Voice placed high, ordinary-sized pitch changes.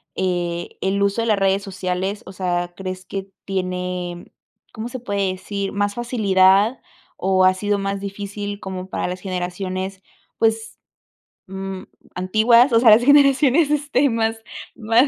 Yes: high, 195 Hz; average, 3.1 semitones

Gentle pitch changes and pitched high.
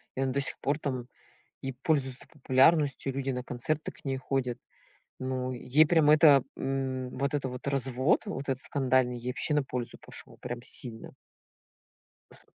No: narrow, 1.8 semitones; low, 135 Hz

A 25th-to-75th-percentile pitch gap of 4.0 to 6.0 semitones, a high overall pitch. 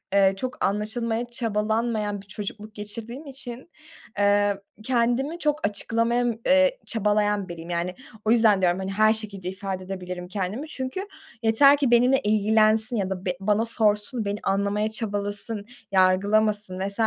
No: average, 2.8 semitones; high, 210 Hz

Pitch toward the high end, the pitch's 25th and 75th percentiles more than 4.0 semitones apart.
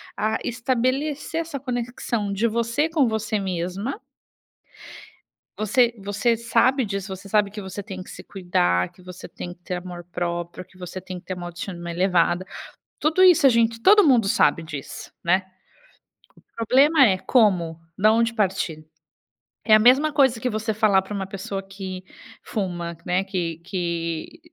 Yes: high, 200 Hz; average, 4.6 semitones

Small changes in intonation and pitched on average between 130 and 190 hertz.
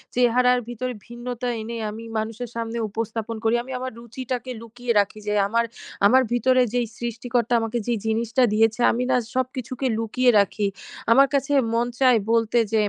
No: narrow, 1.8 semitones; high, 235 Hz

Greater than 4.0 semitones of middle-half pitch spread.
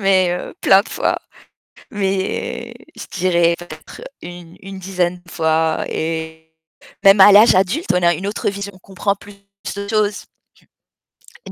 No: narrow, 2.6 semitones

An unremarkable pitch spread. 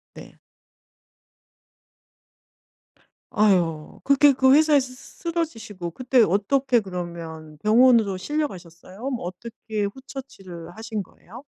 No: wide, 6.7 semitones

